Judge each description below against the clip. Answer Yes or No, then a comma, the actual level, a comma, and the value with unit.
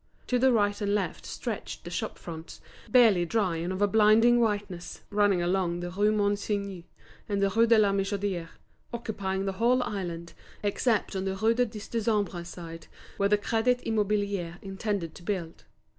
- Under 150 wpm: No, average, 175 wpm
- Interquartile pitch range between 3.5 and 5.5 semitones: No, average, 2.8 semitones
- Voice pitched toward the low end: No, high, 200 Hz